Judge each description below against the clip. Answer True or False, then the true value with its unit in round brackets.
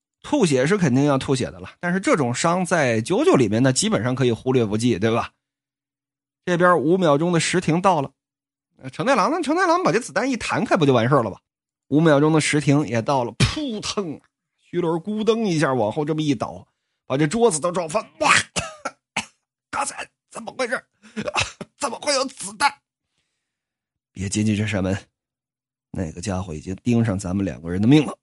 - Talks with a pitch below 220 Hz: True (140 Hz)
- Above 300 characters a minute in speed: False (270 characters per minute)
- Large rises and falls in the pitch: True (6.8 semitones)